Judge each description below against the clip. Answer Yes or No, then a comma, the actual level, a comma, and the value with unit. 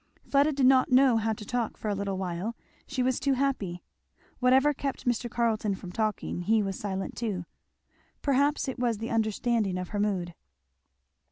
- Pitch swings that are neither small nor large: Yes, average, 4.4 semitones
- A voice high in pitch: Yes, high, 225 Hz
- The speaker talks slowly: No, average, 175 wpm